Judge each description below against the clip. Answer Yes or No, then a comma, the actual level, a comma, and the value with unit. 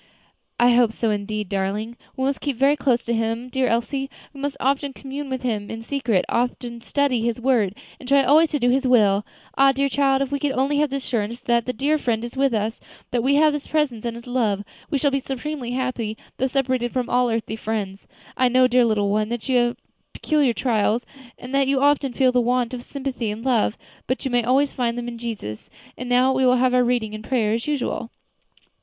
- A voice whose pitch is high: Yes, very high, 250 Hz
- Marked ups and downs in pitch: No, average, 2.9 semitones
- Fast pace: Yes, fast, 225 wpm